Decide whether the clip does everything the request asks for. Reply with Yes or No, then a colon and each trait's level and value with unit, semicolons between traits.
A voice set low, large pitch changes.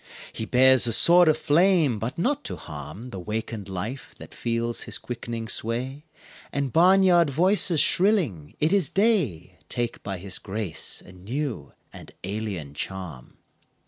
Yes: low, 120 Hz; wide, 8.8 semitones